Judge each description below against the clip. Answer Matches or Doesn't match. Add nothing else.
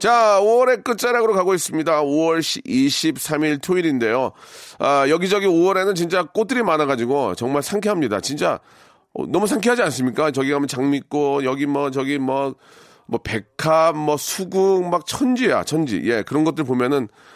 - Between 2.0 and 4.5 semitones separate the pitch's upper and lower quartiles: Doesn't match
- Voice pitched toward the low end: Doesn't match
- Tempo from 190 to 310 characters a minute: Doesn't match